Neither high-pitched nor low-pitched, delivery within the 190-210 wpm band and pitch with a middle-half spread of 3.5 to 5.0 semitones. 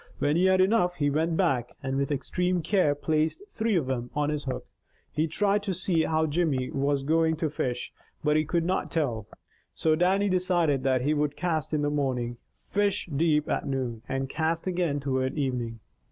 Yes: medium, 155 Hz; average, 195 wpm; average, 4.4 semitones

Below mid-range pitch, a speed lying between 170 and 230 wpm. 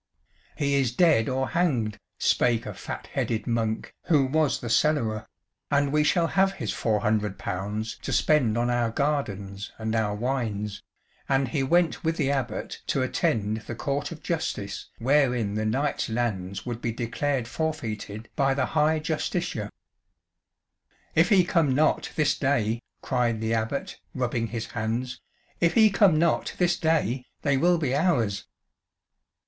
No: low, 125 Hz; average, 155 wpm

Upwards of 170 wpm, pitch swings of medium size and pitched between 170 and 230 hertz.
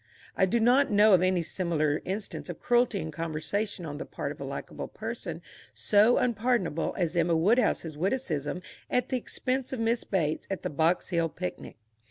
No: average, 180 wpm; wide, 5.8 semitones; medium, 185 Hz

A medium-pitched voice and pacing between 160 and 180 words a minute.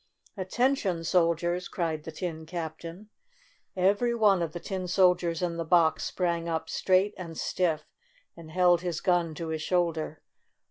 Yes: medium, 175 Hz; average, 170 wpm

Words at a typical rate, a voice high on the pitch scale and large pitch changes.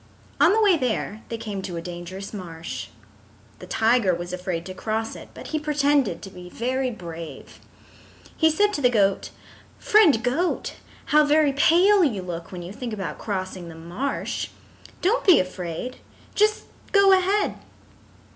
Yes: average, 160 wpm; high, 225 Hz; wide, 8.8 semitones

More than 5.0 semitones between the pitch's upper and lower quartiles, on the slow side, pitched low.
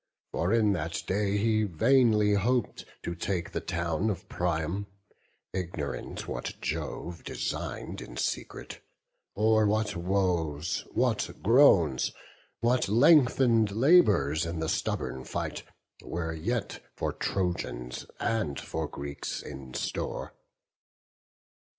Yes: wide, 5.4 semitones; slow, 110 wpm; very low, 95 Hz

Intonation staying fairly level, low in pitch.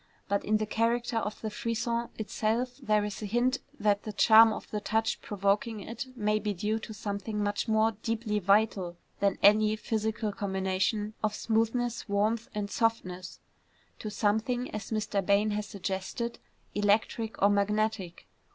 No: narrow, 1.8 semitones; high, 215 Hz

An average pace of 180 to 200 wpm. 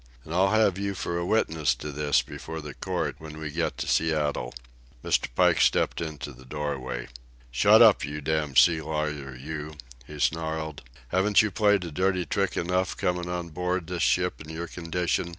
Yes: average, 185 wpm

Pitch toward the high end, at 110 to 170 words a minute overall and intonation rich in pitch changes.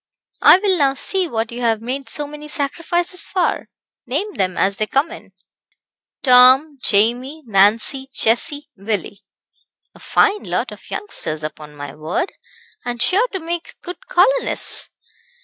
Yes: very high, 270 Hz; average, 145 wpm; wide, 7.8 semitones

